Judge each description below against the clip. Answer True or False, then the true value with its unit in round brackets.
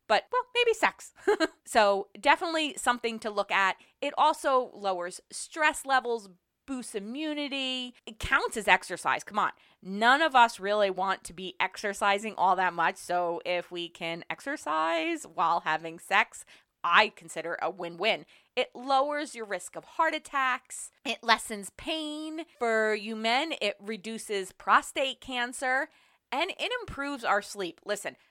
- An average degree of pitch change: False (6.7 semitones)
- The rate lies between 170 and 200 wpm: False (150 wpm)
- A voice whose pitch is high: True (225 Hz)